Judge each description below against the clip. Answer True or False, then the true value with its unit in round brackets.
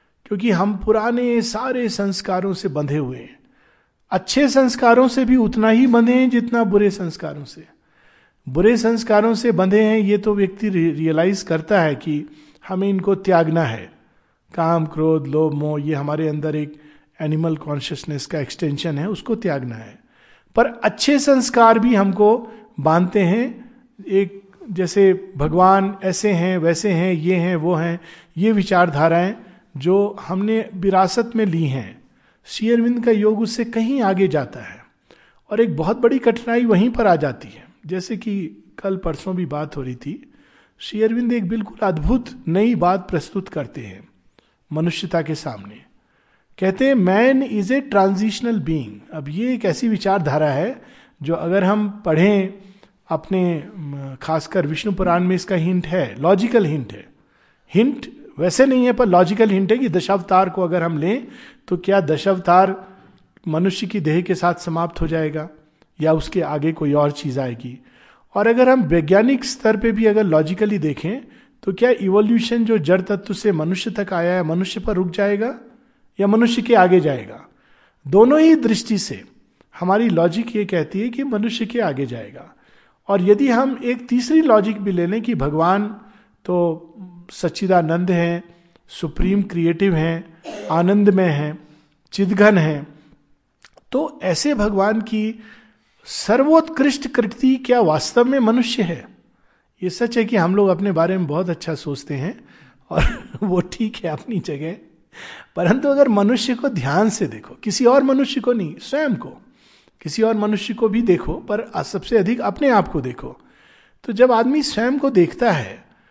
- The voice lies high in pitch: True (195 Hz)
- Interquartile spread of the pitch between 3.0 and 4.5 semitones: False (5.2 semitones)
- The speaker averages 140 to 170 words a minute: True (160 wpm)